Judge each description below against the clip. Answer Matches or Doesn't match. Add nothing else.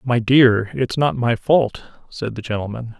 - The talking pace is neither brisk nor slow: Matches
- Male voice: Matches